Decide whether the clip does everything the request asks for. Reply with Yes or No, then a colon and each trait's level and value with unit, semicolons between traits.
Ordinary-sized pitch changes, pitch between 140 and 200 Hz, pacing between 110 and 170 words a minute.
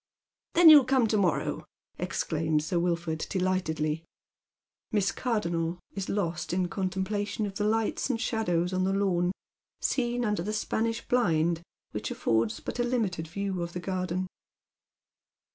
Yes: average, 4.2 semitones; medium, 185 Hz; average, 140 wpm